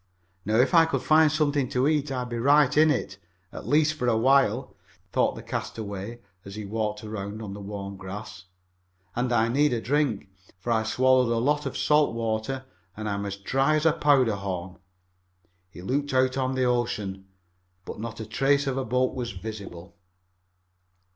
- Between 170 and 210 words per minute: Yes, average, 185 wpm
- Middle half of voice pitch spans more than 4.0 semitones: Yes, average, 4.5 semitones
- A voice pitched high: No, low, 120 Hz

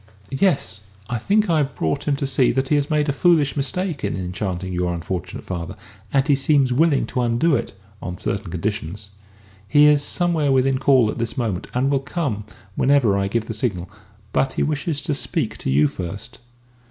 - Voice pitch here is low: Yes, low, 130 Hz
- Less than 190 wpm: No, average, 200 wpm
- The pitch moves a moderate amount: No, wide, 6.6 semitones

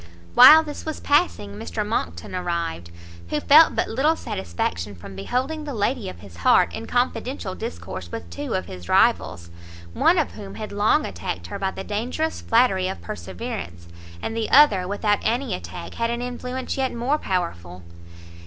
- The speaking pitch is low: No, high, 200 Hz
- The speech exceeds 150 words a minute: Yes, average, 170 wpm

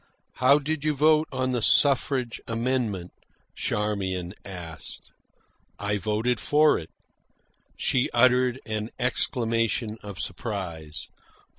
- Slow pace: Yes, slow, 105 wpm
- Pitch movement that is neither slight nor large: Yes, average, 4.1 semitones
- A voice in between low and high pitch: No, low, 115 Hz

